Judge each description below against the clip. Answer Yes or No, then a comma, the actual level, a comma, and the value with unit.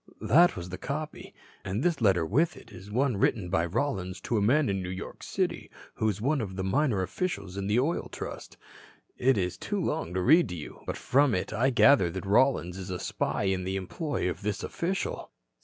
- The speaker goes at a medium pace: No, fast, 215 wpm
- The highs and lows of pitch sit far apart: Yes, wide, 6.9 semitones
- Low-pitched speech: Yes, low, 105 Hz